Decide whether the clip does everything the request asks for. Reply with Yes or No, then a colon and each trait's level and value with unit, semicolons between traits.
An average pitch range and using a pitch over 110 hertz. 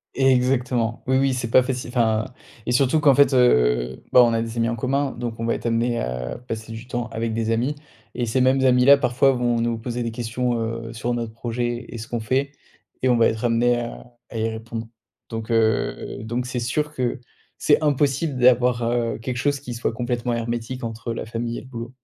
No: narrow, 1.8 semitones; low, 120 Hz